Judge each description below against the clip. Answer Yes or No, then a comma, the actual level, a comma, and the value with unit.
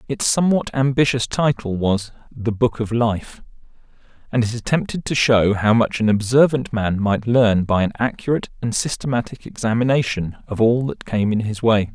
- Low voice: Yes, low, 115 Hz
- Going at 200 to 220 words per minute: No, average, 170 wpm